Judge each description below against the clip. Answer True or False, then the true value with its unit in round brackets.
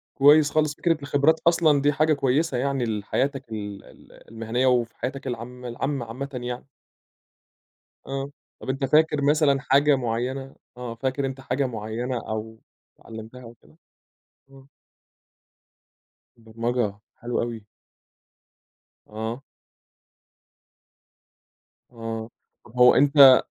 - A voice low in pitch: True (130 Hz)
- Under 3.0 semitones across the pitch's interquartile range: False (3.4 semitones)